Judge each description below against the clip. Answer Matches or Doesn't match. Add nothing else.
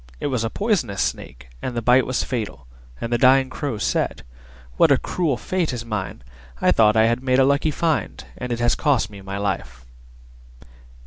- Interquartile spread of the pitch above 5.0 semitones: Doesn't match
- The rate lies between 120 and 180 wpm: Doesn't match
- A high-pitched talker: Doesn't match